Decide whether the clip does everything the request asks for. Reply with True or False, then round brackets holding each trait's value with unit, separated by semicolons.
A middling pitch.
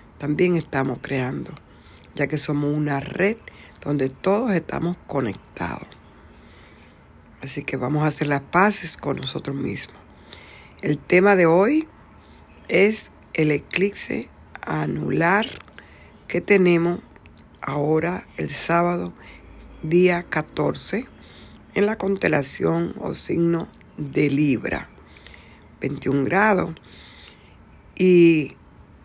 True (145 Hz)